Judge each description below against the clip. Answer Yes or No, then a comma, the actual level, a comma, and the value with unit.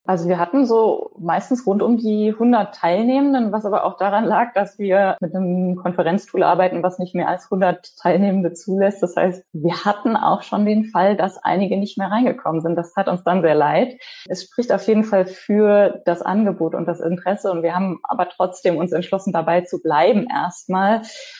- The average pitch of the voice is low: No, high, 190 Hz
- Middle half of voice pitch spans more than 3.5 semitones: No, average, 3.0 semitones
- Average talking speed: No, fast, 195 wpm